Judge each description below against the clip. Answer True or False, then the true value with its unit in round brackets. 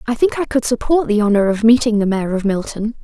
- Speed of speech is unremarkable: False (255 wpm)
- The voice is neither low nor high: False (225 Hz)